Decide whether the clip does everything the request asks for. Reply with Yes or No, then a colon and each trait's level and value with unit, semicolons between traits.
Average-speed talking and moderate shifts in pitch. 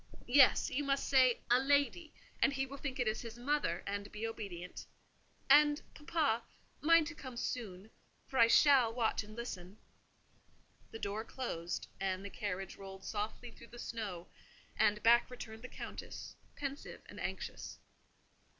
Yes: average, 155 wpm; average, 4.9 semitones